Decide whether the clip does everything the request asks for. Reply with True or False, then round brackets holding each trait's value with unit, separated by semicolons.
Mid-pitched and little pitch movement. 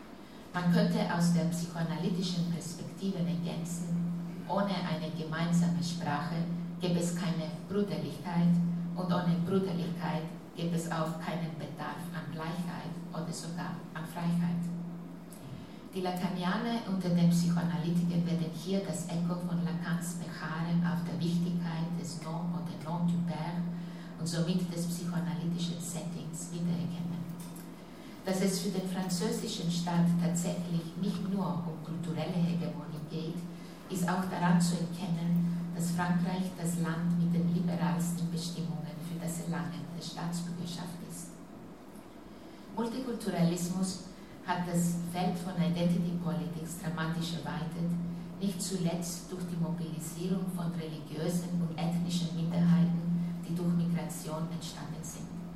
True (175 Hz; 0.8 semitones)